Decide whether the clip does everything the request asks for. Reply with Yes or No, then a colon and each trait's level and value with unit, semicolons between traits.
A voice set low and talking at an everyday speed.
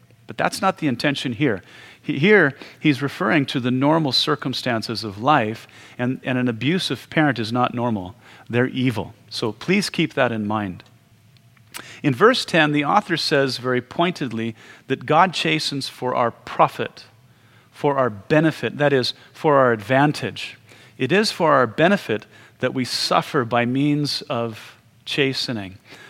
Yes: low, 125 Hz; average, 150 wpm